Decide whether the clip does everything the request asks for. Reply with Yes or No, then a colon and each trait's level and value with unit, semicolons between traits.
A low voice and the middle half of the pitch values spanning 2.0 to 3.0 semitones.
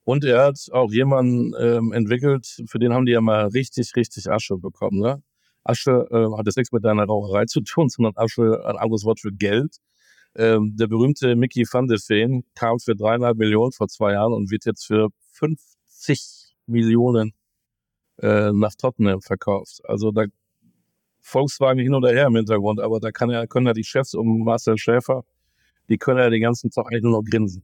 Yes: low, 115 Hz; narrow, 2.4 semitones